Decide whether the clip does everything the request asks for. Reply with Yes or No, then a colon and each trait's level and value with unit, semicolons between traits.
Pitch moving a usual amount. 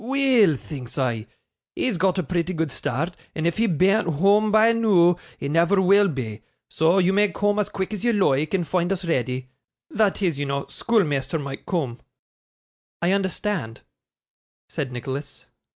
No: wide, 6.3 semitones